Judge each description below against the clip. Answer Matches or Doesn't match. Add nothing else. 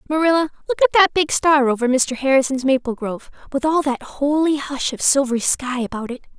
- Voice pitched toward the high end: Matches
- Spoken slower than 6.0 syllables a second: Doesn't match